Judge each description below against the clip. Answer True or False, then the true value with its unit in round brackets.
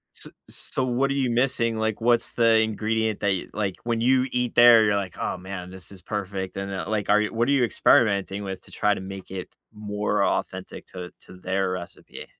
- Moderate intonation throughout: True (3.3 semitones)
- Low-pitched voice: True (105 Hz)